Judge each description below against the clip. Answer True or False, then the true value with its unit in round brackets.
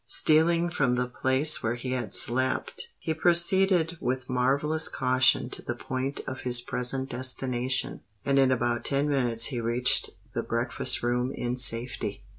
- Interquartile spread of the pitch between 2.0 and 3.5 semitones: True (2.5 semitones)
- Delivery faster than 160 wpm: False (155 wpm)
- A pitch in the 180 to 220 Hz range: False (130 Hz)